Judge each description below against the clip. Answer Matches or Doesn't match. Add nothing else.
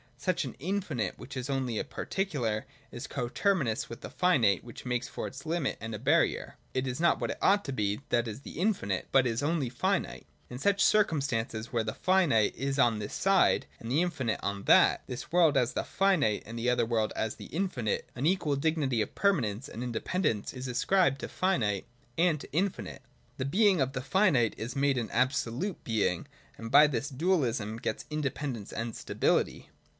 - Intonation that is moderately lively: Doesn't match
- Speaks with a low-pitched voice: Matches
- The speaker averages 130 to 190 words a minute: Doesn't match